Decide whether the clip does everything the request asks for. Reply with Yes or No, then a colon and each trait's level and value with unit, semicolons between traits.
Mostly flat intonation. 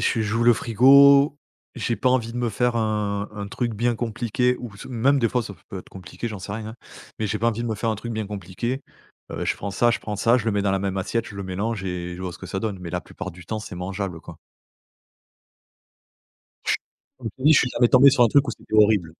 No: average, 3.3 semitones